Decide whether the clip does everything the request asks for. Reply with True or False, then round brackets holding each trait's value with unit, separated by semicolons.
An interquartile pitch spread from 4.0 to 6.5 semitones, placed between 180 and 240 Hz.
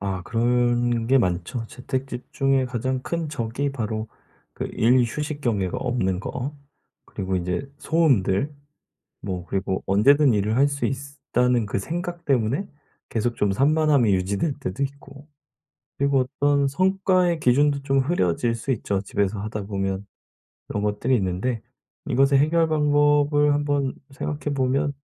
False (5.3 semitones; 130 Hz)